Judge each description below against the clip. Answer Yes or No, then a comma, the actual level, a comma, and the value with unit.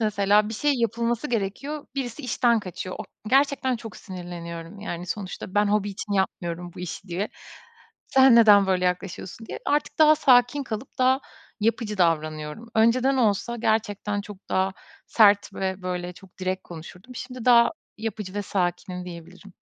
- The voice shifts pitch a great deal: No, average, 4.3 semitones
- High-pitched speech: Yes, high, 205 Hz